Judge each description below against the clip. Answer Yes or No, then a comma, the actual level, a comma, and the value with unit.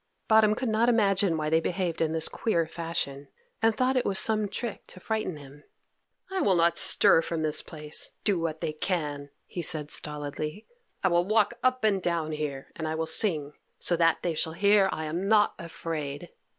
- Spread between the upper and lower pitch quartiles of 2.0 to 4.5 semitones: No, average, 4.9 semitones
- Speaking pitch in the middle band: Yes, medium, 170 Hz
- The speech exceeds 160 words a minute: Yes, average, 195 wpm